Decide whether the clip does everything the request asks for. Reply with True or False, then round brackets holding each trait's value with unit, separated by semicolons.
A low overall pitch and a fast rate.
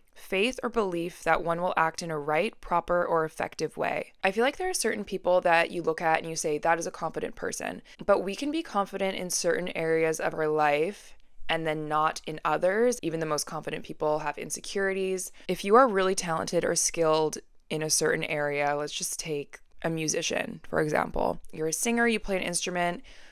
False (170 Hz; 210 wpm)